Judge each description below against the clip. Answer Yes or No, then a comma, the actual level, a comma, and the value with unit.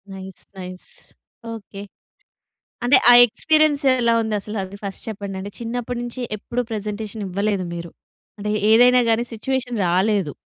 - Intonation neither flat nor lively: Yes, average, 3.5 semitones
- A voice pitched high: Yes, high, 215 Hz